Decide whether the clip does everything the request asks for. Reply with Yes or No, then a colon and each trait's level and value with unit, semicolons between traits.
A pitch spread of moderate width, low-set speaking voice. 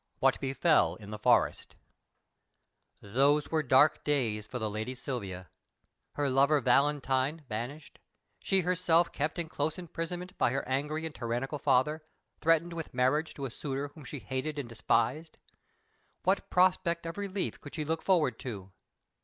No: average, 4.4 semitones; medium, 145 Hz